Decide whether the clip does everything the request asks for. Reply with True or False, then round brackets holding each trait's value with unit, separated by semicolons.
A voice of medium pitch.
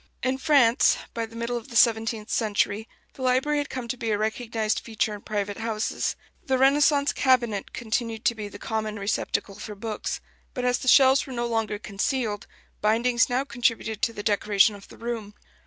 False (230 Hz)